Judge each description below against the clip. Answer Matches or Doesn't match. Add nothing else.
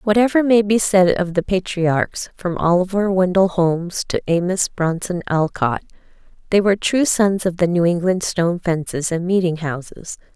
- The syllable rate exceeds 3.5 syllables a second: Matches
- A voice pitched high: Doesn't match